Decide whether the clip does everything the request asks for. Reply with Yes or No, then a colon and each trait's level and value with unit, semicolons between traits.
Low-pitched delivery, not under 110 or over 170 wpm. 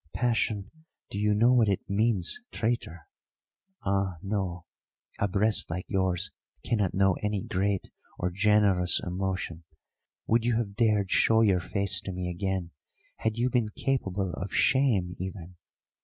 Yes: low, 100 Hz; average, 140 wpm